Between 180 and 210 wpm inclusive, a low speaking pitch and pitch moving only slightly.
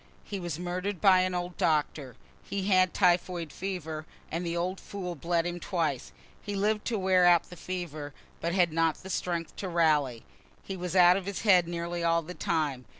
No: average, 190 wpm; medium, 175 Hz; narrow, 2.0 semitones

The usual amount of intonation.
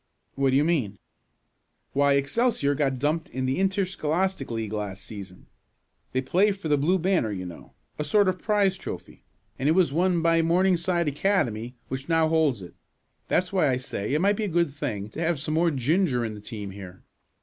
No: wide, 6.3 semitones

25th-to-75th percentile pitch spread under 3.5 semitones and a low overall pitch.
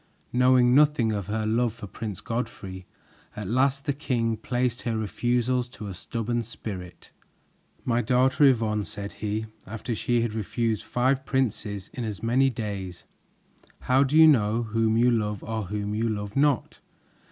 Yes: average, 2.9 semitones; low, 115 Hz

